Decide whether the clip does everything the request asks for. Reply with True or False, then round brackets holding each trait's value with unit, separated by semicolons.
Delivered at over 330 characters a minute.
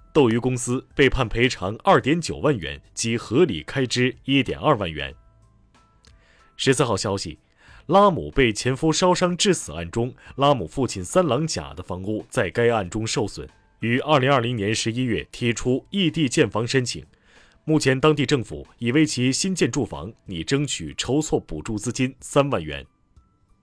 False (245 characters per minute)